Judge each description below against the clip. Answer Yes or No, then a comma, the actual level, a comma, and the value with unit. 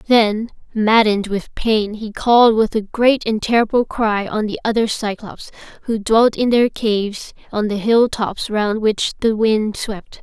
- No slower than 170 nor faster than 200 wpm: Yes, average, 175 wpm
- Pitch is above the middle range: Yes, high, 220 Hz